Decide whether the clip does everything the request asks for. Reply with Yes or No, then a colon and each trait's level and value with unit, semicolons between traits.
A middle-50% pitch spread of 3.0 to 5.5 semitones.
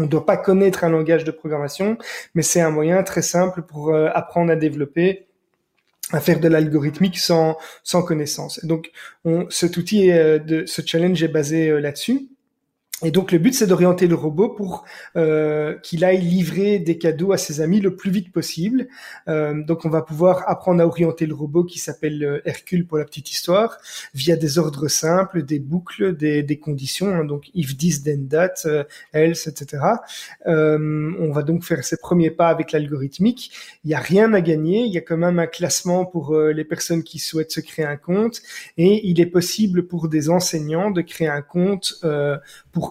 No: narrow, 2.6 semitones